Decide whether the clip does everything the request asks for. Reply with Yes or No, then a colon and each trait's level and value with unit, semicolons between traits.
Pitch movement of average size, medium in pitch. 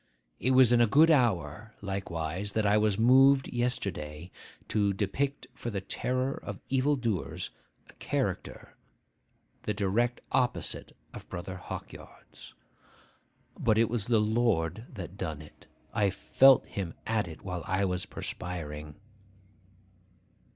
No: average, 5.0 semitones; low, 105 Hz